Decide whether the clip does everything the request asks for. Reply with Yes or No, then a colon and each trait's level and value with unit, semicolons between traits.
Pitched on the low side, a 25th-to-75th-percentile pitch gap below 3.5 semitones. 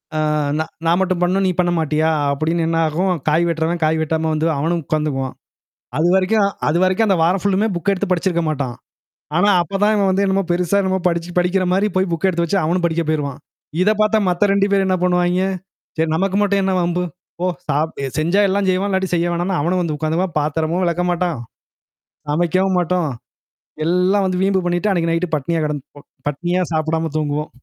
No: medium, 175 Hz; average, 2.9 semitones